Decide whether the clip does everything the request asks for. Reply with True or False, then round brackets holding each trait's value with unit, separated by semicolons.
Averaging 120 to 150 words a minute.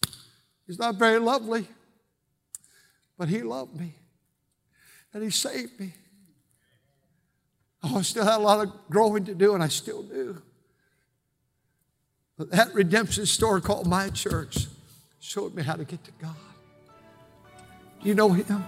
True (140 wpm)